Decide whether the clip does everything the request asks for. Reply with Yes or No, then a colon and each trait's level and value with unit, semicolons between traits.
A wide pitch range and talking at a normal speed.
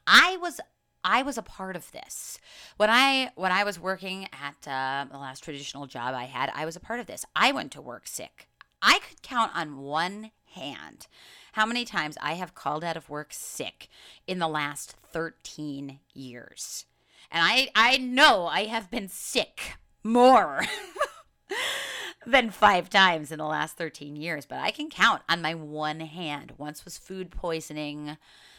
Yes: wide, 7.2 semitones; average, 175 wpm